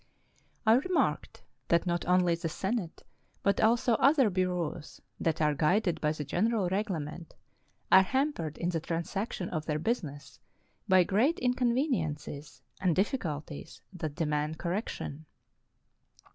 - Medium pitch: Yes, medium, 180 Hz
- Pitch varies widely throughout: Yes, wide, 5.7 semitones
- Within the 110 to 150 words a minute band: Yes, slow, 135 wpm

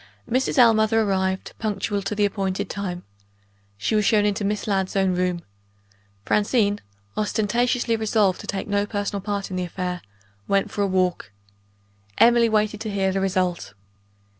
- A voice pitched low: No, high, 200 Hz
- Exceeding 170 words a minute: No, average, 155 wpm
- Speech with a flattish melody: Yes, narrow, 2.1 semitones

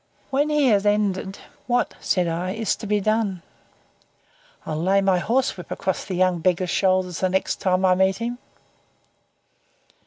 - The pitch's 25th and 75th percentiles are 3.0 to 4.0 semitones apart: No, narrow, 2.6 semitones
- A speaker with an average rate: Yes, average, 155 wpm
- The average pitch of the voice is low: No, high, 190 Hz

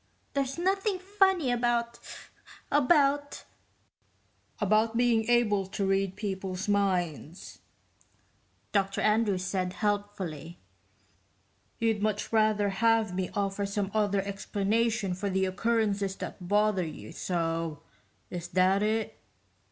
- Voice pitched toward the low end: No, high, 205 Hz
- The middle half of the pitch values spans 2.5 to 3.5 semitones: Yes, average, 3.2 semitones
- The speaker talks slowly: Yes, slow, 105 wpm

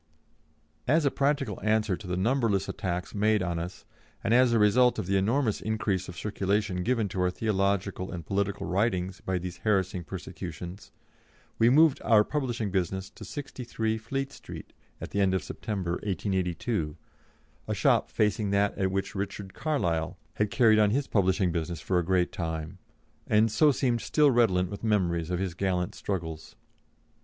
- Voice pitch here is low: Yes, low, 100 Hz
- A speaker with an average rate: Yes, average, 165 wpm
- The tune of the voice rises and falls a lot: No, average, 3.5 semitones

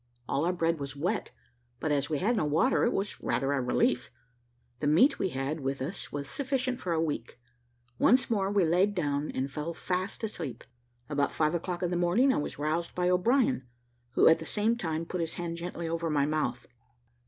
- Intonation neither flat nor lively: Yes, average, 4.5 semitones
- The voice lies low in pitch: No, medium, 165 Hz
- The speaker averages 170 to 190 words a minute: No, fast, 205 wpm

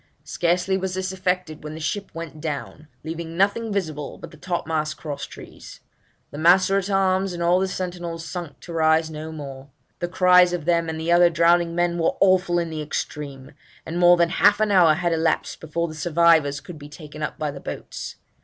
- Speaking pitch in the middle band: Yes, medium, 170 Hz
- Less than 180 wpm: No, fast, 205 wpm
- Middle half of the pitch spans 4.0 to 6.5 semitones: No, narrow, 2.5 semitones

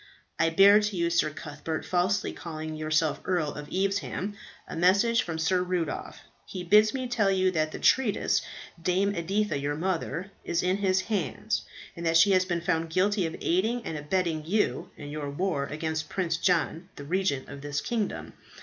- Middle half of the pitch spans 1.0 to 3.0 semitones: No, average, 3.7 semitones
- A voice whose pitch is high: No, medium, 175 Hz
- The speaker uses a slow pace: No, average, 180 wpm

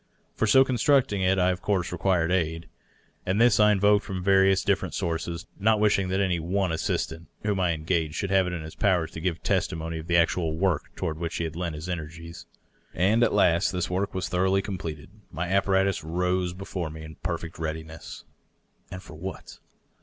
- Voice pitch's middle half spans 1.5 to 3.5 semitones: Yes, average, 2.9 semitones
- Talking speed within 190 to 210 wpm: Yes, average, 200 wpm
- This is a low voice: Yes, very low, 90 Hz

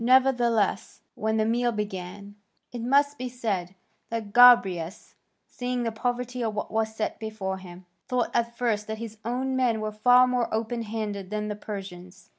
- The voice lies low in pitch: No, high, 220 Hz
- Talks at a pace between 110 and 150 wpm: No, average, 170 wpm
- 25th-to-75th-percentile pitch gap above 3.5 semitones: No, average, 2.9 semitones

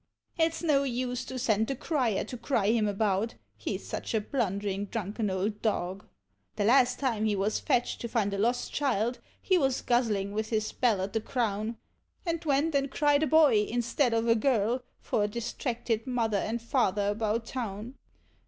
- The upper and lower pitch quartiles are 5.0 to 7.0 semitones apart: No, average, 3.5 semitones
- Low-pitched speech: No, high, 230 Hz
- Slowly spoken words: No, average, 190 wpm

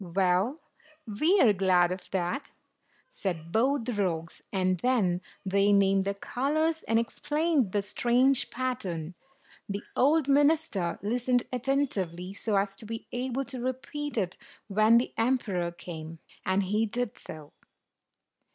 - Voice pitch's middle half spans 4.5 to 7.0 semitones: Yes, wide, 5.6 semitones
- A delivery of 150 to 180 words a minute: No, slow, 135 wpm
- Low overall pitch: No, high, 215 Hz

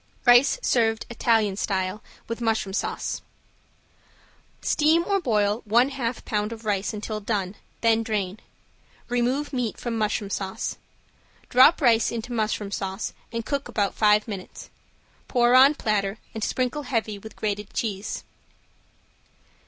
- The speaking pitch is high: Yes, high, 225 Hz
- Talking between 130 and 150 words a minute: Yes, slow, 135 wpm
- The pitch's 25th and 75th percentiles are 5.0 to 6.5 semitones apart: No, average, 2.8 semitones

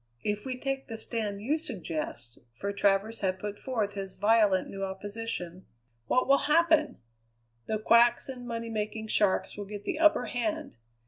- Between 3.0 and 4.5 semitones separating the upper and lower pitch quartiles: Yes, average, 4.1 semitones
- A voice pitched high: Yes, high, 220 Hz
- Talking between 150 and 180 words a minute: Yes, average, 165 wpm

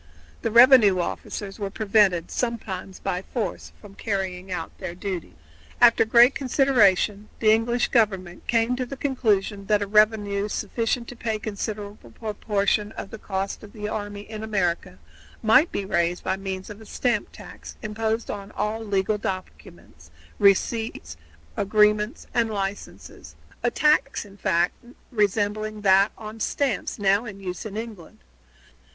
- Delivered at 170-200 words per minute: No, average, 145 wpm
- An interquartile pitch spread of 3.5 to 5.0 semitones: No, narrow, 2.5 semitones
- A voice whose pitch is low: No, high, 210 Hz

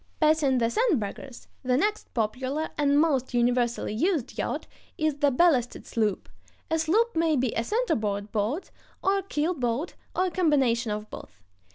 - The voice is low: No, very high, 275 Hz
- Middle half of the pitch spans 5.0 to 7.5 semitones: Yes, wide, 5.6 semitones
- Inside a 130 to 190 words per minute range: Yes, average, 170 wpm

